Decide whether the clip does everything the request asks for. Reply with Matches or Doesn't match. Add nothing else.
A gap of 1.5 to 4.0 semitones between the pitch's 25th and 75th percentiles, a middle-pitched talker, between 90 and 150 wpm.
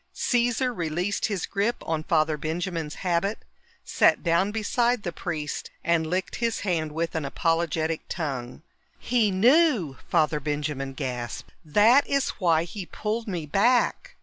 Doesn't match